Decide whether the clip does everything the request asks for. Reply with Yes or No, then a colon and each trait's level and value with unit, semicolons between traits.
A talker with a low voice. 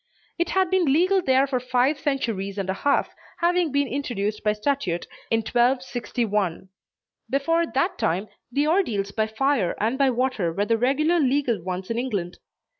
No: very high, 250 Hz